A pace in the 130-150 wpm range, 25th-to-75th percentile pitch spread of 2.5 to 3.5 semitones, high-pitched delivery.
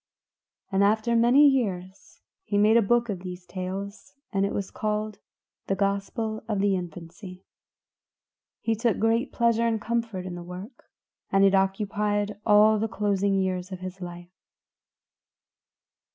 Yes: average, 145 wpm; average, 2.9 semitones; high, 200 Hz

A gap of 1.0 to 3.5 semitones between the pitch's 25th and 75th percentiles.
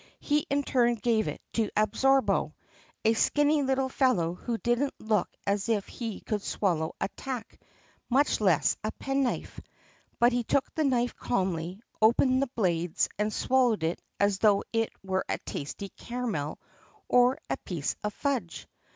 No: average, 4.6 semitones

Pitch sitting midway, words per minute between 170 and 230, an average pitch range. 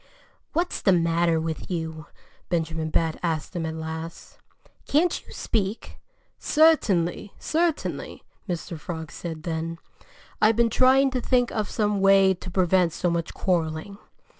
No: medium, 175 Hz; average, 140 wpm; average, 4.7 semitones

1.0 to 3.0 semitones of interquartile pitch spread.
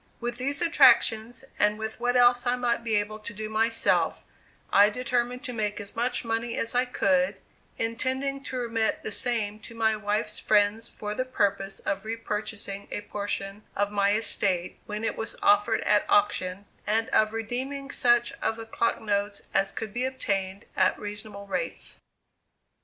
Yes: average, 2.7 semitones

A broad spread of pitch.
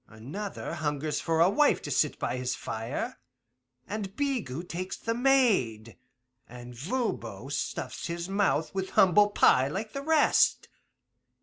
Yes: wide, 8.4 semitones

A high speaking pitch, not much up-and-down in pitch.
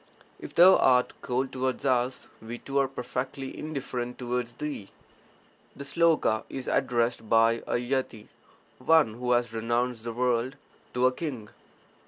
No: low, 125 Hz; narrow, 2.2 semitones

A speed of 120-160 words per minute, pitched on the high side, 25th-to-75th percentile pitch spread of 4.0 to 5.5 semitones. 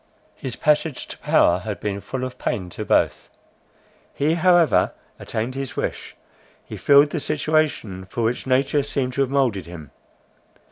No: average, 155 wpm; low, 135 Hz; average, 4.7 semitones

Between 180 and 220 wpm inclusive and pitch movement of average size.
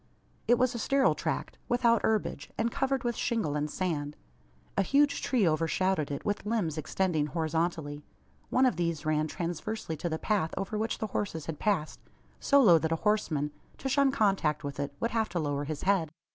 No: average, 190 wpm; wide, 6.5 semitones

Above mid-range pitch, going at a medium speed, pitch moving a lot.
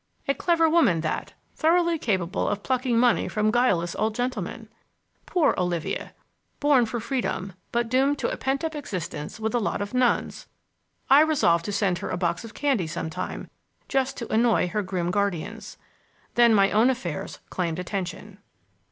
Yes: high, 220 Hz; average, 165 wpm; wide, 6.1 semitones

